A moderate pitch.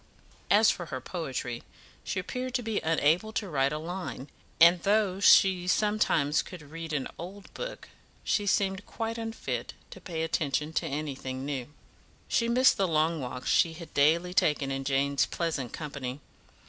Yes: medium, 165 Hz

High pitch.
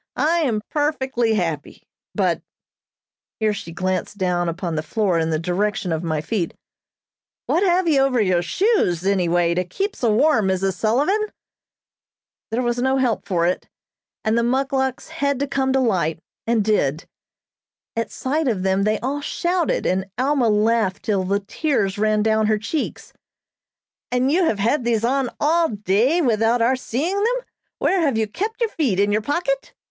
Yes: high, 225 Hz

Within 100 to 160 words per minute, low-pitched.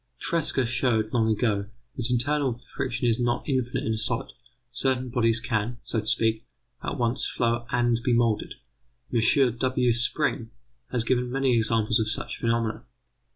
Yes: average, 155 wpm; low, 120 Hz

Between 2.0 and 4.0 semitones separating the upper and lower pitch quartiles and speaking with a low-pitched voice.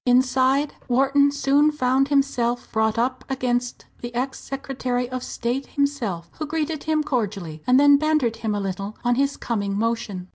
No: average, 3.5 semitones; very high, 255 Hz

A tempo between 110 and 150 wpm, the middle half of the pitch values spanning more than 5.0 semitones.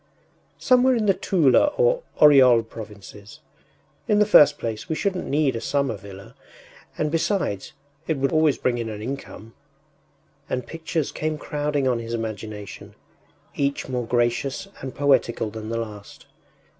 Yes: average, 145 wpm; wide, 5.5 semitones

